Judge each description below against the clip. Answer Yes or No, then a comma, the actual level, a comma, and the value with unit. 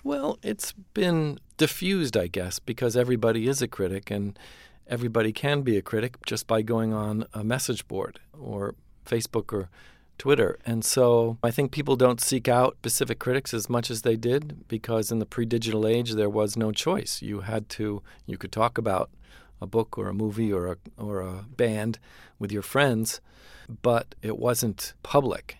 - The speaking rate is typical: Yes, average, 180 wpm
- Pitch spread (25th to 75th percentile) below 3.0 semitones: Yes, narrow, 2.5 semitones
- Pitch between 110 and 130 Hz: Yes, low, 115 Hz